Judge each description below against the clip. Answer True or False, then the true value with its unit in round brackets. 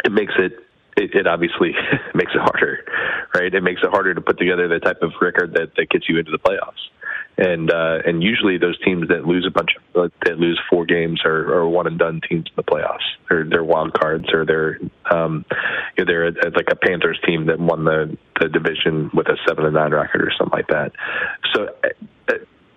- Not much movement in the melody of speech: True (1.2 semitones)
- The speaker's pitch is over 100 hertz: False (85 Hz)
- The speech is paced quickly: True (220 wpm)